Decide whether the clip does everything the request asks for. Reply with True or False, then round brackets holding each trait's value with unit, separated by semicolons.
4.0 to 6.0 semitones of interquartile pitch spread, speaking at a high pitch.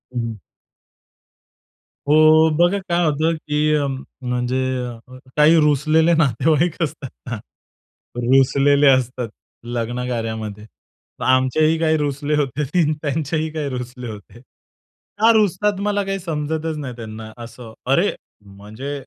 False (4.3 semitones; 145 Hz)